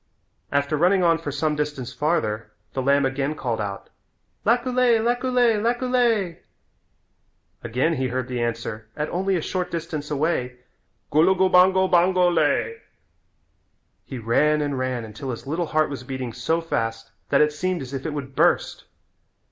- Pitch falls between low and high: Yes, medium, 150 Hz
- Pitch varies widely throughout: Yes, wide, 6.0 semitones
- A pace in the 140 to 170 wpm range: Yes, average, 150 wpm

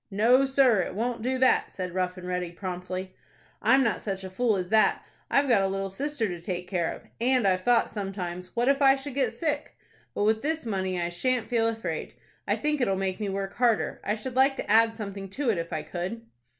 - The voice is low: No, high, 210 Hz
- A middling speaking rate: No, fast, 230 wpm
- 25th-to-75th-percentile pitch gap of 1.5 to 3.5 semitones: No, average, 5.2 semitones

